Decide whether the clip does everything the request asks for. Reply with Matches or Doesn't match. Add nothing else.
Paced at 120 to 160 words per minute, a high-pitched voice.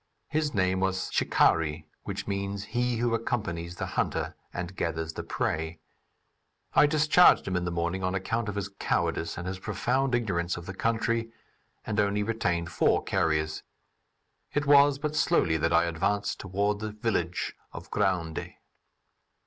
Doesn't match